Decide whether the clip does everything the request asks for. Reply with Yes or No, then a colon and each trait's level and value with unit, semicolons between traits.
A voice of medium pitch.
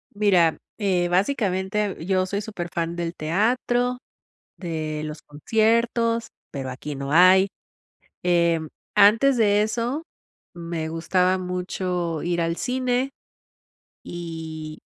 Yes: medium, 180 Hz